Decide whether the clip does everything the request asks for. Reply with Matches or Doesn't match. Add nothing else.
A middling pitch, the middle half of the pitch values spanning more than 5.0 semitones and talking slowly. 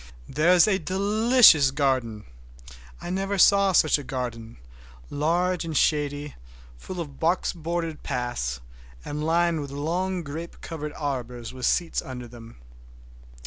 Matches